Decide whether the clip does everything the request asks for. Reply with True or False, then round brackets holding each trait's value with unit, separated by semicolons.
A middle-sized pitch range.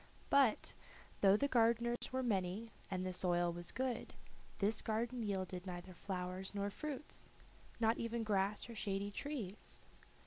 True (4.1 semitones)